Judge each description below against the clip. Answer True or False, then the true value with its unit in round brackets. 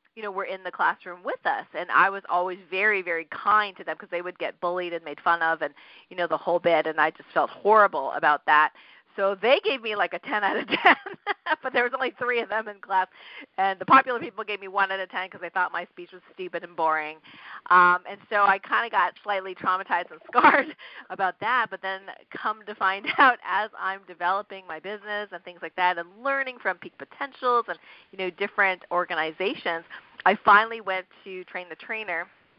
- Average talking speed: False (225 wpm)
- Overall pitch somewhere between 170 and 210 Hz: True (190 Hz)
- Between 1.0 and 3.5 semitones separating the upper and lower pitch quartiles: True (3.0 semitones)